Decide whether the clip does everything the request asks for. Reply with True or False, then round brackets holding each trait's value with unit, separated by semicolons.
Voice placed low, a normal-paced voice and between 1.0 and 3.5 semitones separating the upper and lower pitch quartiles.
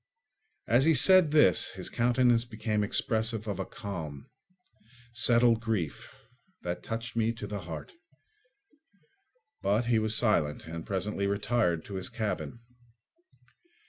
False (110 Hz; 125 wpm; 3.1 semitones)